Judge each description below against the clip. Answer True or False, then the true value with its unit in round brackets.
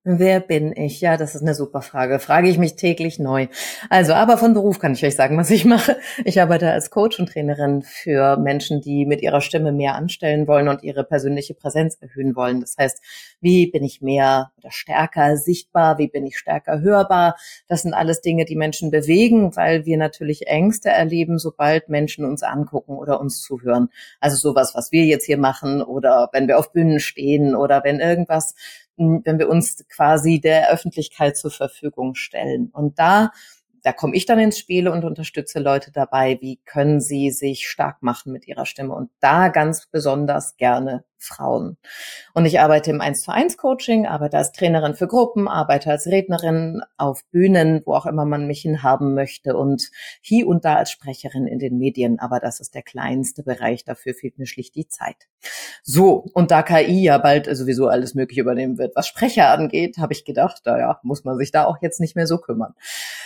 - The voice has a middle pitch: True (150 Hz)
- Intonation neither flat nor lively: True (3.5 semitones)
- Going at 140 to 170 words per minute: False (190 wpm)